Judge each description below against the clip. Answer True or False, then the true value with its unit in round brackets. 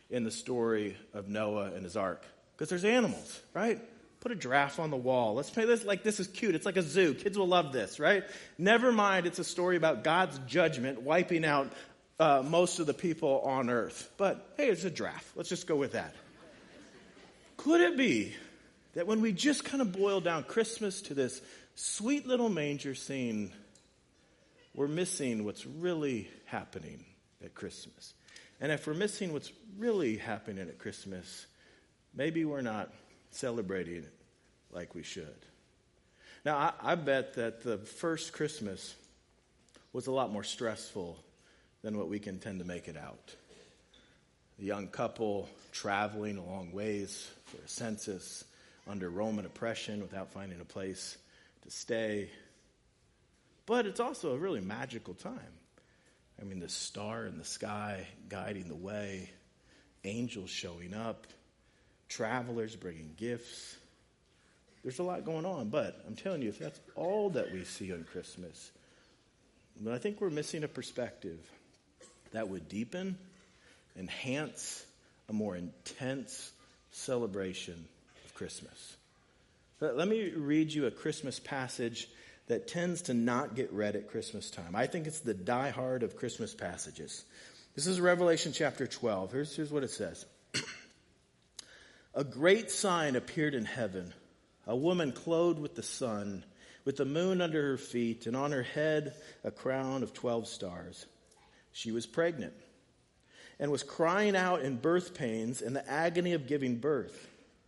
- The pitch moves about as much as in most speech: False (8.8 semitones)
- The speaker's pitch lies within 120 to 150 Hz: True (135 Hz)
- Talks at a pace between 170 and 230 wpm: False (155 wpm)